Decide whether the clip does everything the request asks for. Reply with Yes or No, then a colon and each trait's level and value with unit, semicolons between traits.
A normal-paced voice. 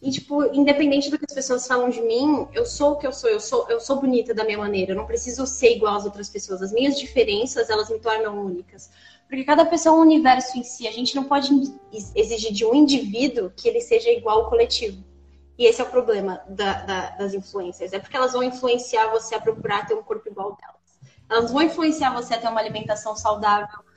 No: fast, 235 wpm